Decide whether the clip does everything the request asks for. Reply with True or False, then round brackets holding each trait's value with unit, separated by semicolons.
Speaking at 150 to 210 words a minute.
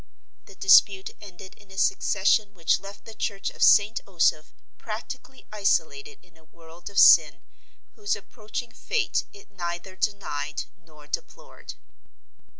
False (135 wpm)